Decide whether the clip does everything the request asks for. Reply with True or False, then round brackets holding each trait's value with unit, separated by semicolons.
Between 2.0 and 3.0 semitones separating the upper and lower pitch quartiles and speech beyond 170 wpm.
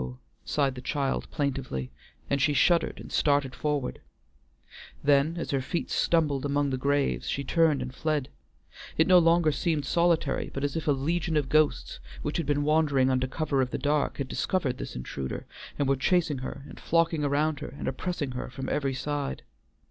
True (2.7 semitones; 185 wpm)